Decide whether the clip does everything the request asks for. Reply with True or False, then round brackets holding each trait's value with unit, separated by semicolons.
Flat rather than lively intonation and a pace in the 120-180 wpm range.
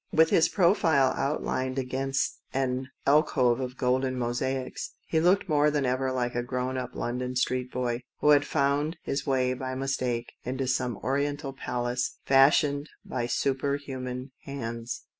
True (1.9 semitones; 150 wpm)